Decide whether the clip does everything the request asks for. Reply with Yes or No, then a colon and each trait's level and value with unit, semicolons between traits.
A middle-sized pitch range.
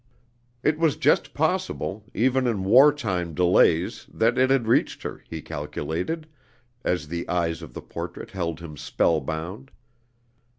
No: wide, 8.1 semitones